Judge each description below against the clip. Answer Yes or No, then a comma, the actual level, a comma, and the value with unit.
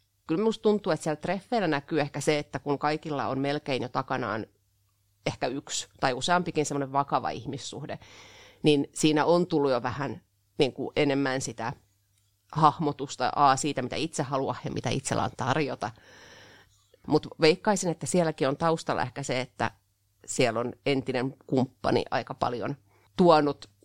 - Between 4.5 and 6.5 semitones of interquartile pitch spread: Yes, average, 4.8 semitones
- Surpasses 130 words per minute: Yes, average, 150 wpm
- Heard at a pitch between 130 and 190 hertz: Yes, medium, 140 Hz